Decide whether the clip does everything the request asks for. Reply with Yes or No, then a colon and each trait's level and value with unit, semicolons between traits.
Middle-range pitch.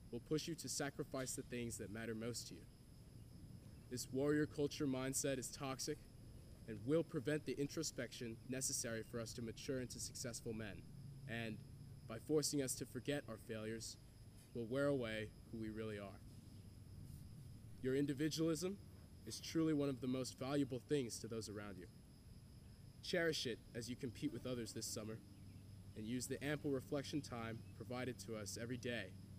No: low, 120 Hz